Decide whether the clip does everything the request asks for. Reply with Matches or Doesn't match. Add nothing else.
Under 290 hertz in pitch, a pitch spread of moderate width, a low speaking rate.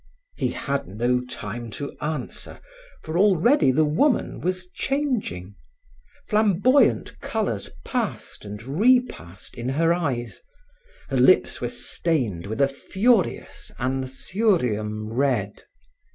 Doesn't match